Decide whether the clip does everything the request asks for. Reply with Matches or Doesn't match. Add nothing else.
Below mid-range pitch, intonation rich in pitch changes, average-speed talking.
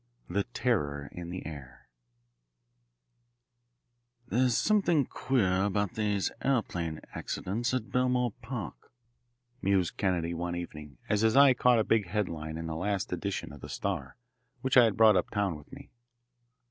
Matches